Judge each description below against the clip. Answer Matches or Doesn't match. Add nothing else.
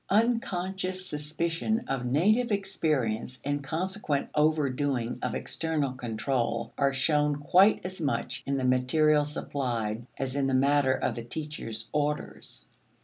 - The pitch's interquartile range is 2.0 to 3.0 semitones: Doesn't match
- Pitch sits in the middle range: Matches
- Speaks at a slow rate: Matches